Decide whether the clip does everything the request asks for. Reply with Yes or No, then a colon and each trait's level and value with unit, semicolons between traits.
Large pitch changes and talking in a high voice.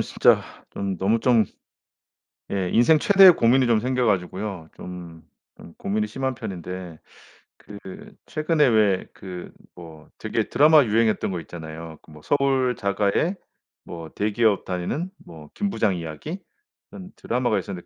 No: wide, 6.1 semitones; low, 105 Hz